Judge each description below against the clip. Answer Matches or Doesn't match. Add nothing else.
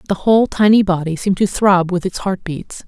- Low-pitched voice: Doesn't match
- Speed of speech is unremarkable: Doesn't match